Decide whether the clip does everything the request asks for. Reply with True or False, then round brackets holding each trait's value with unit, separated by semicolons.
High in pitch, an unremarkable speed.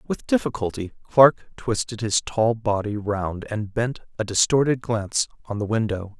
False (110 Hz; 155 wpm)